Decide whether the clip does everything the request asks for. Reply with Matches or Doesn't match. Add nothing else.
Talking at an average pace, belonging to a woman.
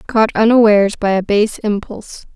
Matches